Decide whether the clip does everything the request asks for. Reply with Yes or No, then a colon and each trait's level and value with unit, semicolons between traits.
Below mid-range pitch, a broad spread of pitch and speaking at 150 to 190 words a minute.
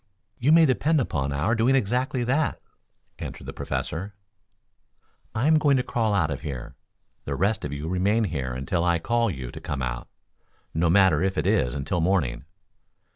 Yes: very low, 95 Hz; wide, 8.2 semitones; average, 180 wpm